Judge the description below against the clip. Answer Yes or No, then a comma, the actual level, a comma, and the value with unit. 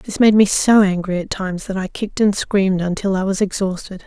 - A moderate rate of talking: No, fast, 235 wpm